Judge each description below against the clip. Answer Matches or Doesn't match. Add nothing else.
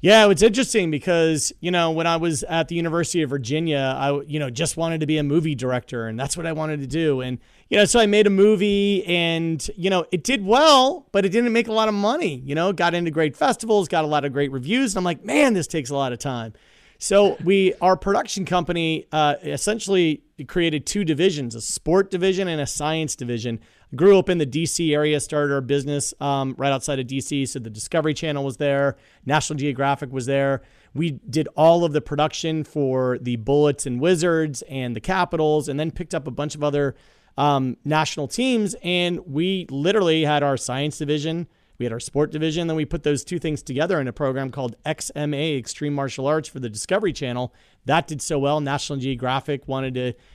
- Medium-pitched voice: Matches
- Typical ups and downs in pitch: Matches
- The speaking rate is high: Matches